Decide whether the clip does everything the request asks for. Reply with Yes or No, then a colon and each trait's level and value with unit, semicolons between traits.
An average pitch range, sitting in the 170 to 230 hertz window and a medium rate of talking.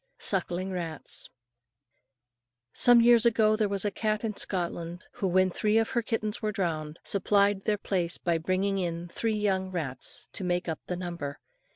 Yes: average, 3.5 semitones; high, 190 Hz; average, 170 wpm